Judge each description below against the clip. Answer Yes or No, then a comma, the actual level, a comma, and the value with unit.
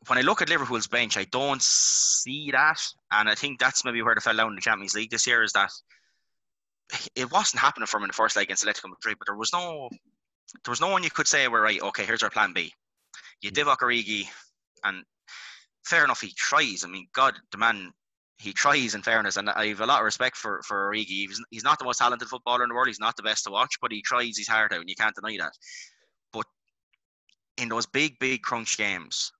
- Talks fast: Yes, fast, 240 wpm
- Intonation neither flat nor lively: Yes, average, 3.2 semitones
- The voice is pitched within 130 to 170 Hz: No, low, 115 Hz